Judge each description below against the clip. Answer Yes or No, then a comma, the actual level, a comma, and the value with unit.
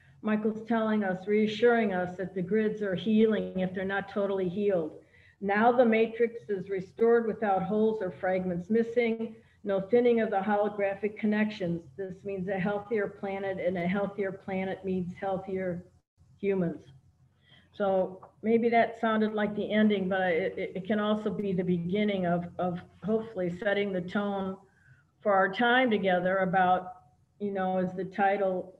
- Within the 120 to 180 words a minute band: Yes, average, 155 wpm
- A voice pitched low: No, high, 195 Hz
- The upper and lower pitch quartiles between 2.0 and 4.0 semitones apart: Yes, narrow, 2.4 semitones